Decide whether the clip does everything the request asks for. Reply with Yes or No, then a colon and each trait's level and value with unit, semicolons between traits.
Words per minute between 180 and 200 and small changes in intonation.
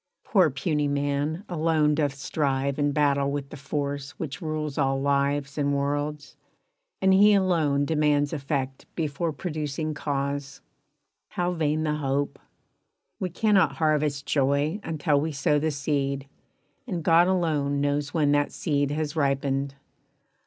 No: average, 140 wpm; narrow, 1.9 semitones